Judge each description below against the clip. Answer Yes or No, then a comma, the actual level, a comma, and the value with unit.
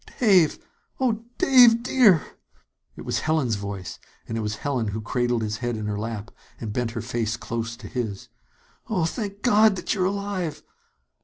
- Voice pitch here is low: Yes, low, 125 Hz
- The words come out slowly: No, average, 170 wpm